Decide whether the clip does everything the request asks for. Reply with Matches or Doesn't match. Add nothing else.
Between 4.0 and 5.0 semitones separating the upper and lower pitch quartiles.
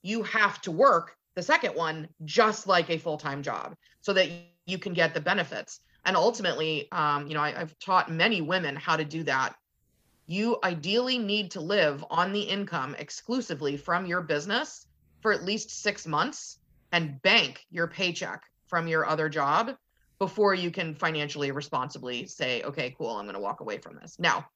Matches